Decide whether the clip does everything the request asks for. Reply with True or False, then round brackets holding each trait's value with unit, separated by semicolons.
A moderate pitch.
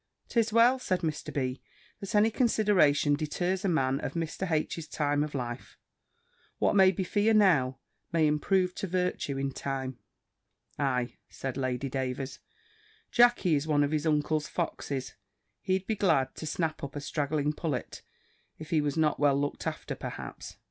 True (155 Hz)